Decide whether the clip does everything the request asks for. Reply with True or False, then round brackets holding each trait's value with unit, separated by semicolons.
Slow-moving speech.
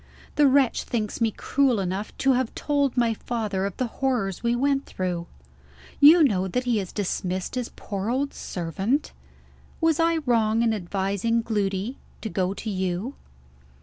False (160 wpm)